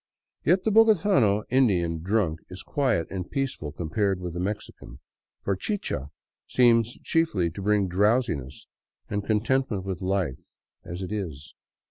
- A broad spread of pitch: Yes, wide, 5.7 semitones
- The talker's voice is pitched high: No, low, 100 Hz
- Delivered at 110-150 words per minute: Yes, average, 140 wpm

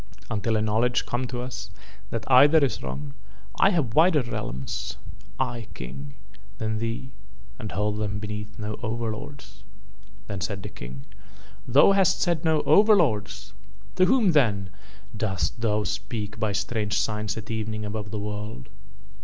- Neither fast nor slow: Yes, average, 145 wpm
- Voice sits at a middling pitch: No, low, 110 Hz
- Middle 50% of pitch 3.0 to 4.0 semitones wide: Yes, average, 3.5 semitones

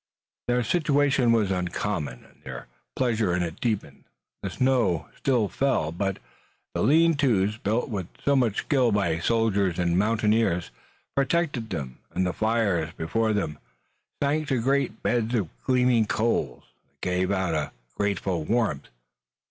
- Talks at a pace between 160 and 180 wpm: No, average, 145 wpm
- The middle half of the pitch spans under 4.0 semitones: No, wide, 5.6 semitones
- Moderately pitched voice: No, low, 110 Hz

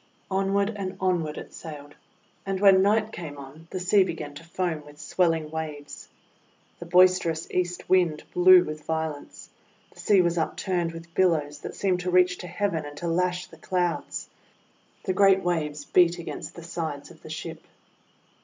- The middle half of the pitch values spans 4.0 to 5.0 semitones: No, average, 2.7 semitones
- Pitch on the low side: No, medium, 175 Hz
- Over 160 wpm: Yes, average, 175 wpm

